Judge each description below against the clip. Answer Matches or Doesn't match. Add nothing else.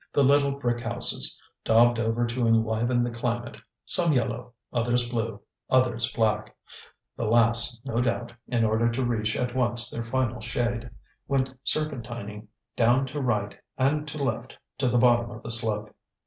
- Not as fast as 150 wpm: Doesn't match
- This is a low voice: Matches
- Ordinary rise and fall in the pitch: Doesn't match